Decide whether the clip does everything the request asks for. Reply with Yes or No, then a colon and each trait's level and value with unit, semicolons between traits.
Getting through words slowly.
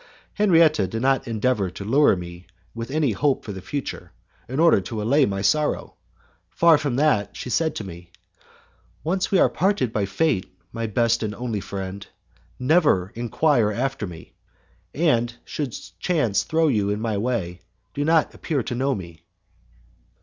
No: average, 165 wpm